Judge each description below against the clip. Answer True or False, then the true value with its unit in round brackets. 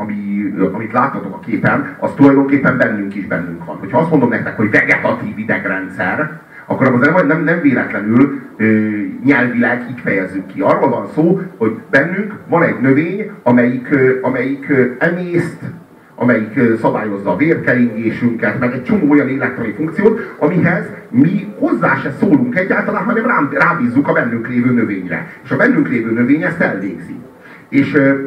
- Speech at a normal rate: True (145 wpm)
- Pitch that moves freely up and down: True (6.4 semitones)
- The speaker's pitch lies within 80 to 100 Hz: False (130 Hz)